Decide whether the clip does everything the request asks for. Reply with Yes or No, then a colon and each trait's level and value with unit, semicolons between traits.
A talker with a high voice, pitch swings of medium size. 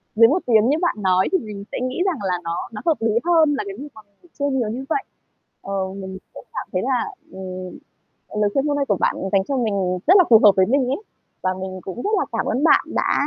No: high, 230 Hz; wide, 6.9 semitones